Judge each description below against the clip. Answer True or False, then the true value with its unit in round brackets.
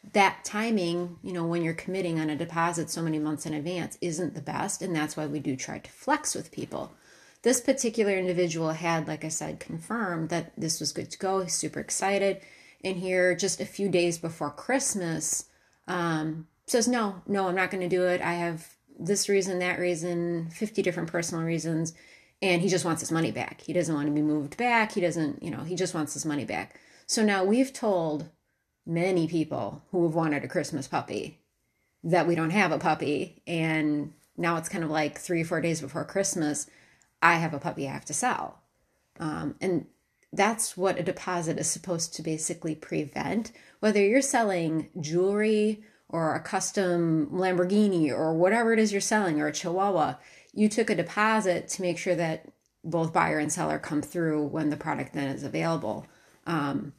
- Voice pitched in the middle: True (170 Hz)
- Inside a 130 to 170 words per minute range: False (195 wpm)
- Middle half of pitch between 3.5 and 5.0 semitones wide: False (3.0 semitones)